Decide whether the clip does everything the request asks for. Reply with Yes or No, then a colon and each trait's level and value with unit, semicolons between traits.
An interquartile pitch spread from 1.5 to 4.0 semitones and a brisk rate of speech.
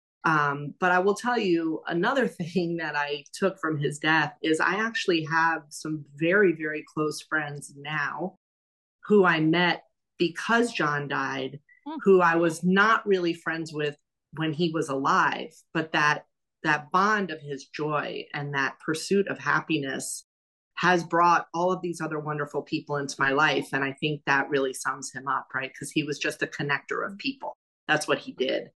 No: average, 3.4 semitones; average, 175 wpm